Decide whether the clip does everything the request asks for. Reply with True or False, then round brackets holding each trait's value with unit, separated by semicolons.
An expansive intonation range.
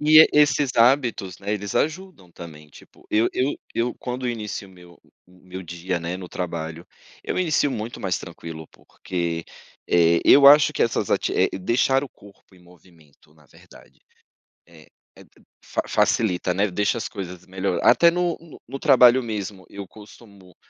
True (6.0 semitones)